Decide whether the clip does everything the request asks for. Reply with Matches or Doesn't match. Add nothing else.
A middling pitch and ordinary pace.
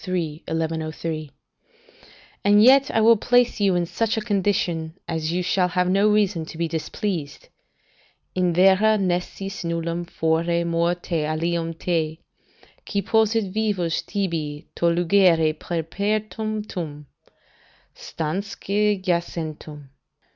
Doesn't match